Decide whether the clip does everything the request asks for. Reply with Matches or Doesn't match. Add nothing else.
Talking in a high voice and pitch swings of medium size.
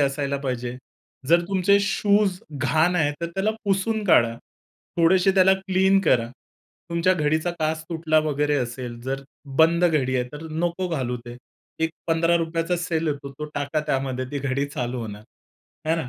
Doesn't match